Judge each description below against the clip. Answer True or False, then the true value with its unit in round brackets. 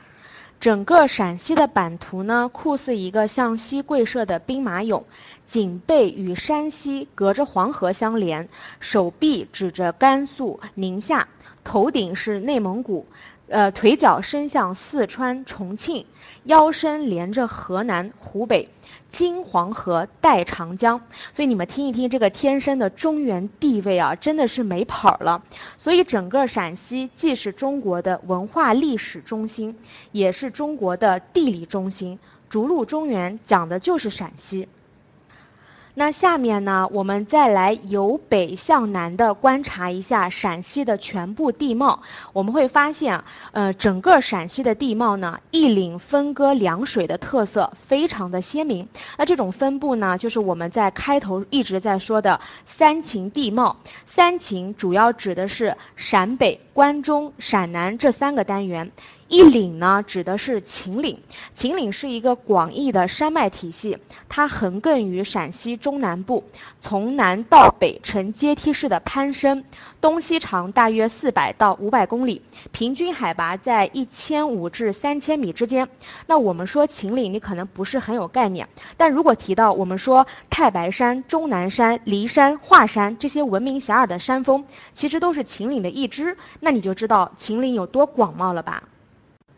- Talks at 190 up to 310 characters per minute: True (235 characters per minute)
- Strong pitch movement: True (6.2 semitones)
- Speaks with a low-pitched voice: False (230 Hz)